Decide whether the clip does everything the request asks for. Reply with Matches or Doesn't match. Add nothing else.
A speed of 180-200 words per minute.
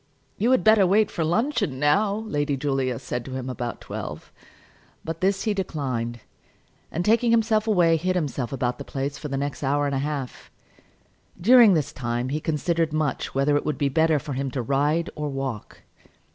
Matches